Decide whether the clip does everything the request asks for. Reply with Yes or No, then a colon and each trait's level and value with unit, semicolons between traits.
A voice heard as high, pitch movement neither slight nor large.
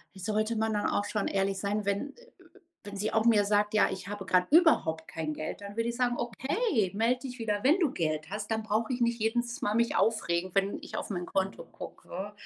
Yes: high, 210 Hz; average, 3.3 semitones